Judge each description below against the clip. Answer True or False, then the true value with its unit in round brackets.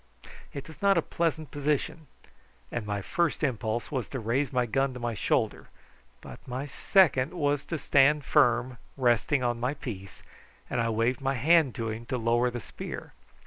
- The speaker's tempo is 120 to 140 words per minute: False (180 wpm)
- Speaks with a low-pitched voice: True (130 Hz)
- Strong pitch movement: False (3.7 semitones)